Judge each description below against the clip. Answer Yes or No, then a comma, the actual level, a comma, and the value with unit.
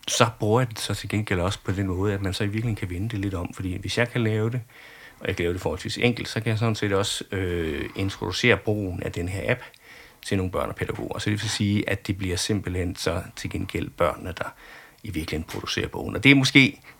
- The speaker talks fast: Yes, fast, 260 wpm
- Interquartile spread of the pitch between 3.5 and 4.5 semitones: No, average, 3.0 semitones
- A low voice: Yes, low, 105 Hz